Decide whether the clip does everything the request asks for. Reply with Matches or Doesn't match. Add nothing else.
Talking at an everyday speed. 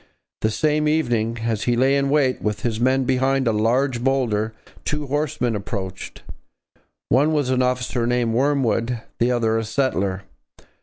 Matches